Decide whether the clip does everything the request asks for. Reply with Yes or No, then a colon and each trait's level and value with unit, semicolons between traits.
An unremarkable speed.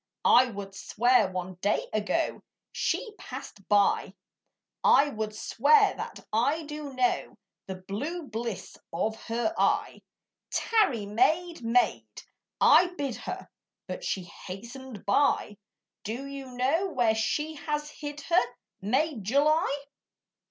No: slow, 125 wpm